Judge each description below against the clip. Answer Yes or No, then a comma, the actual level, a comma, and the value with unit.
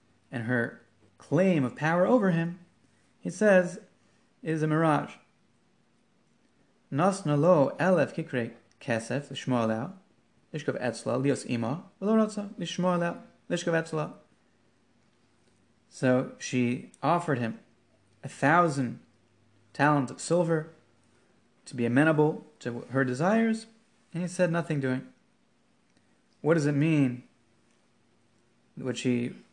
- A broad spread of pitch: Yes, wide, 6.3 semitones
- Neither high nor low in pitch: Yes, medium, 150 Hz